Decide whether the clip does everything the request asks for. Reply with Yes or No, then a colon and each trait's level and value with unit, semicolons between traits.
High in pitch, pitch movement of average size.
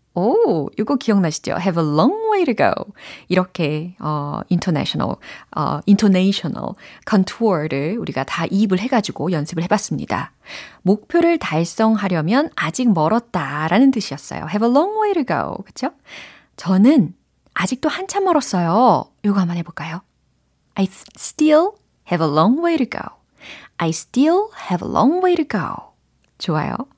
No: high, 205 Hz; wide, 8.7 semitones